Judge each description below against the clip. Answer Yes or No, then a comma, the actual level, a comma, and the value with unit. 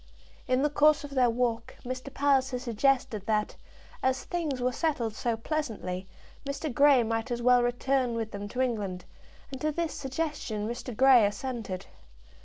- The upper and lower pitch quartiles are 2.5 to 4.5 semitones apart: Yes, average, 3.3 semitones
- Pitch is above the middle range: Yes, very high, 250 Hz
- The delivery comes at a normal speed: Yes, average, 160 wpm